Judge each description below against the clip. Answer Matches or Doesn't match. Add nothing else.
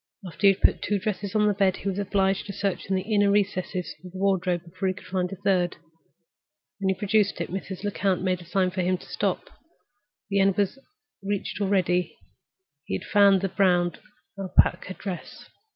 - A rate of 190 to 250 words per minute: Matches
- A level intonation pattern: Matches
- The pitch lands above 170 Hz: Matches